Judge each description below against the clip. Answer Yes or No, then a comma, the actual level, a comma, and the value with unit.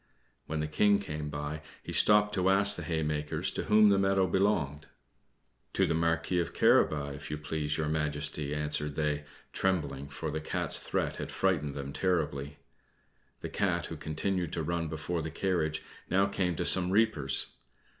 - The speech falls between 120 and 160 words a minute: No, average, 170 wpm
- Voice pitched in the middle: No, very low, 80 Hz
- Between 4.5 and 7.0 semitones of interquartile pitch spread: No, average, 3.8 semitones